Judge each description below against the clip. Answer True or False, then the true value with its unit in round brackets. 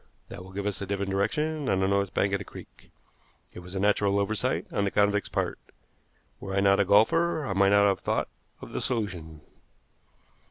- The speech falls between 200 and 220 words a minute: True (205 wpm)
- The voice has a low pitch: True (100 Hz)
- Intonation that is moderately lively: False (1.1 semitones)